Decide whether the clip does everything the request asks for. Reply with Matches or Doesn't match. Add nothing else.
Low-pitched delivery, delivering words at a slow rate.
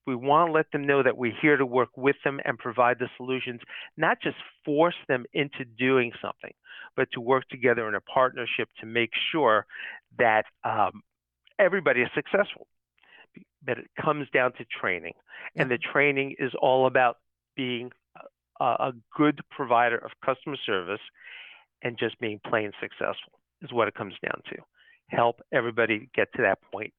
Doesn't match